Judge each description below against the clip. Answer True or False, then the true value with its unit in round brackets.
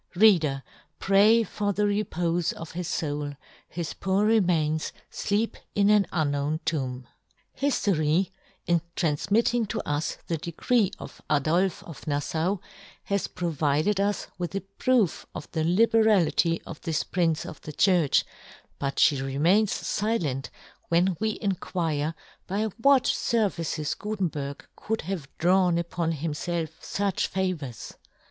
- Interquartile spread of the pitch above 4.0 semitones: True (4.7 semitones)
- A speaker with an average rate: False (130 wpm)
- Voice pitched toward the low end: False (175 Hz)